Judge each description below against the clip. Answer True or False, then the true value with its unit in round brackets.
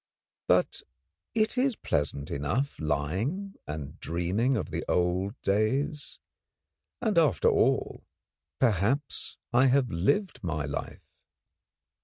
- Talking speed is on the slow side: True (105 wpm)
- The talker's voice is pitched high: False (110 Hz)